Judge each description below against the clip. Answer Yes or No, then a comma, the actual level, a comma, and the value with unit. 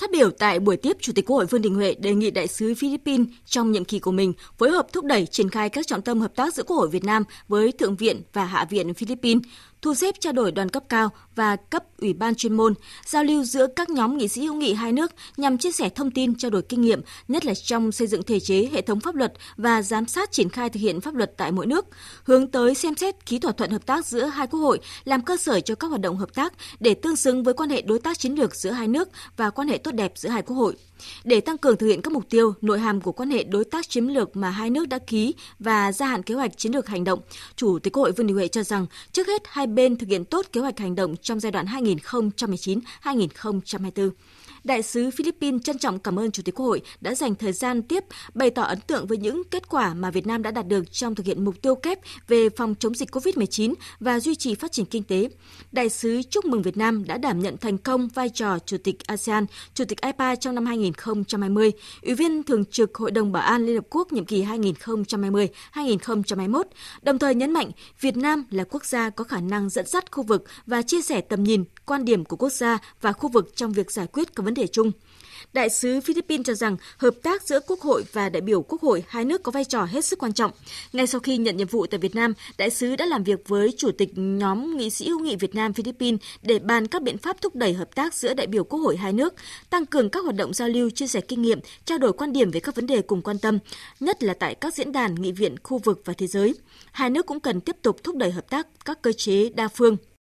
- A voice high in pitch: Yes, high, 230 Hz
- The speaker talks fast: Yes, fast, 260 wpm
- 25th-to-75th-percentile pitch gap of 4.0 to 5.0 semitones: Yes, average, 4.7 semitones